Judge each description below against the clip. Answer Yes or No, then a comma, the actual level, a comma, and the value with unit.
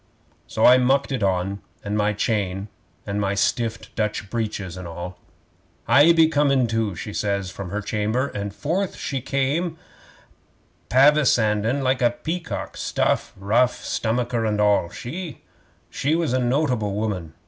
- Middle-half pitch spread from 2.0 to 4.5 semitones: No, average, 5.0 semitones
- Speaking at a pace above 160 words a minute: No, average, 145 wpm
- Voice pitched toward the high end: No, low, 115 Hz